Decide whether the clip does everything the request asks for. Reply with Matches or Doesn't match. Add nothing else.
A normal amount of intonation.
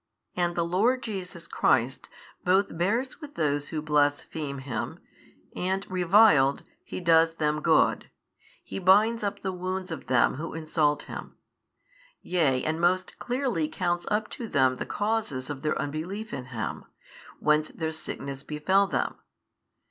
Matches